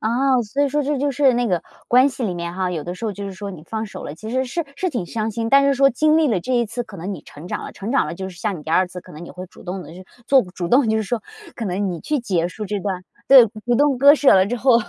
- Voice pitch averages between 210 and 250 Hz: Yes, high, 220 Hz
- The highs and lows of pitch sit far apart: Yes, wide, 6.0 semitones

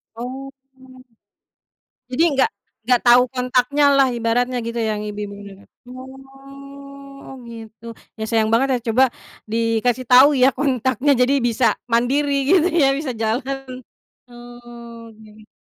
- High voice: Yes, very high, 250 Hz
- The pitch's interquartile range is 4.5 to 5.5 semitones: No, average, 2.8 semitones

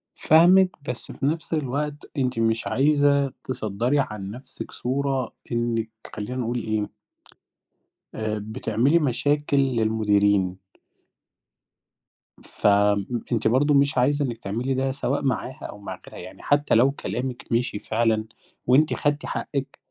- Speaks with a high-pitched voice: No, low, 125 Hz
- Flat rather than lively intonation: No, average, 4.3 semitones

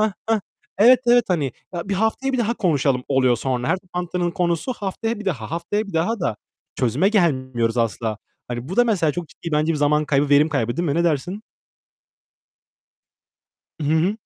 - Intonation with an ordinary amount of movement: No, wide, 6.4 semitones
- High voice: No, medium, 170 Hz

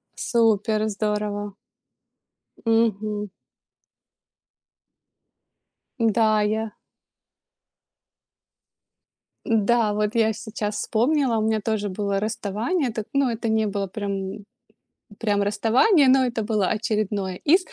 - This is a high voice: Yes, high, 215 Hz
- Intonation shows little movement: Yes, narrow, 1.8 semitones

